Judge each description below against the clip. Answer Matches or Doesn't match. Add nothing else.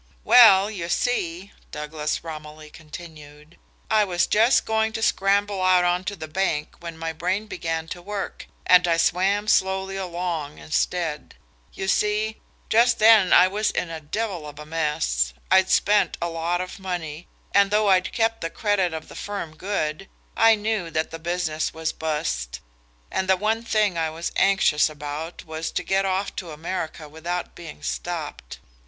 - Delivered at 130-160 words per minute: Doesn't match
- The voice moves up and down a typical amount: Matches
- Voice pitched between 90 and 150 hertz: Doesn't match